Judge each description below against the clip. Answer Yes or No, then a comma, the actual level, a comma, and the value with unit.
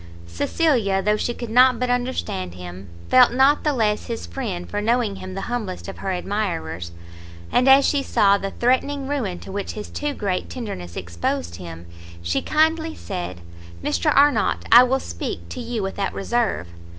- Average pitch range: No, wide, 6.3 semitones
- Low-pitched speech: No, high, 210 Hz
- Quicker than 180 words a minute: No, average, 175 wpm